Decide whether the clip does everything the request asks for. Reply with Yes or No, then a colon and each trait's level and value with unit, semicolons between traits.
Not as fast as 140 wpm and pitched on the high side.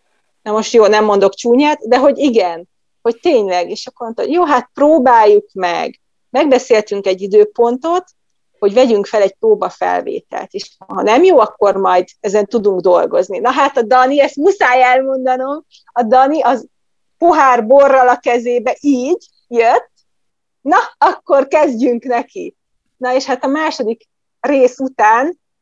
No: average, 145 wpm; very high, 250 Hz